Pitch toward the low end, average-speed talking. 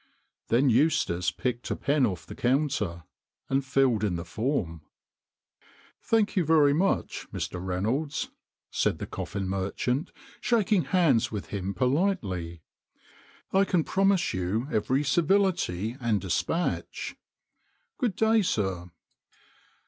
No: low, 130 Hz; slow, 125 wpm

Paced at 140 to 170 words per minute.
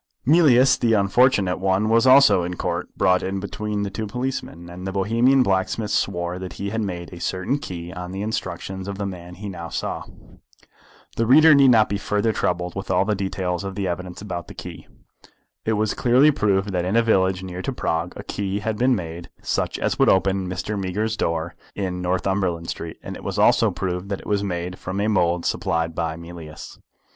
No: fast, 205 wpm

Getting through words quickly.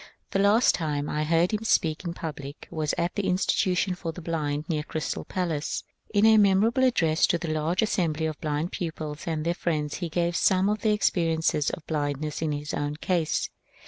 Yes: fast, 210 wpm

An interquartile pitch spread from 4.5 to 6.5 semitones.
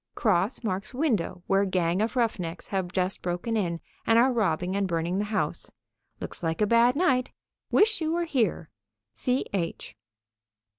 Yes: wide, 5.4 semitones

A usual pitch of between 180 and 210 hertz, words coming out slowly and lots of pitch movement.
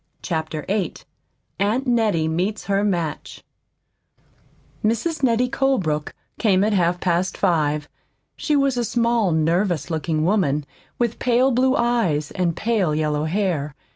Yes: high, 190 Hz; slow, 130 wpm; wide, 6.8 semitones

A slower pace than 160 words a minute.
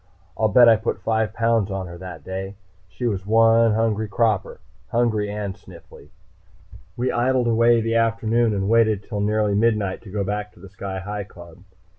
No: average, 180 wpm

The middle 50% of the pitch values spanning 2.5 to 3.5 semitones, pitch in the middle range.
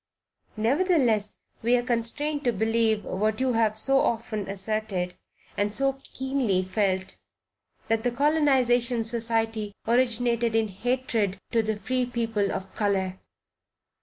No: average, 2.9 semitones; high, 225 Hz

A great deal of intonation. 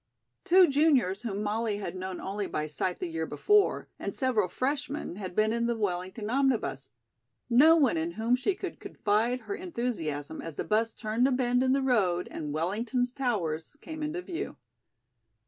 Yes: wide, 6.0 semitones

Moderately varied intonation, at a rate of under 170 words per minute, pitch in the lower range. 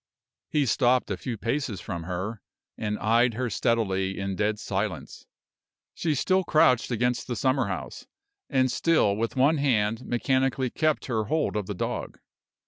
Yes: average, 4.2 semitones; average, 155 wpm; low, 115 Hz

